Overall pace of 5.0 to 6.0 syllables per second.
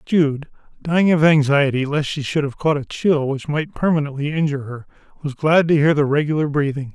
Yes: 5.5 syllables/s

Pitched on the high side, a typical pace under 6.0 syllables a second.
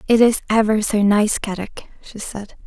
Yes: high, 215 Hz; 4.9 syllables/s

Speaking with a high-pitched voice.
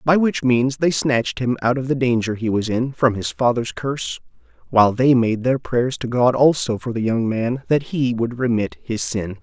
No: low, 125 Hz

